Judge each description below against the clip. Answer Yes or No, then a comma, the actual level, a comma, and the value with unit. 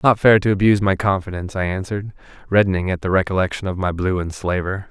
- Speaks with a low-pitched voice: Yes, very low, 95 Hz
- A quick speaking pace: Yes, fast, 210 wpm